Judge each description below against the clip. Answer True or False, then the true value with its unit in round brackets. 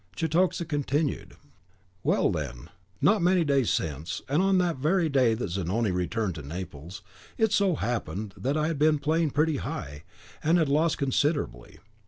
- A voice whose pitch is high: False (140 Hz)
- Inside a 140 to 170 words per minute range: True (160 wpm)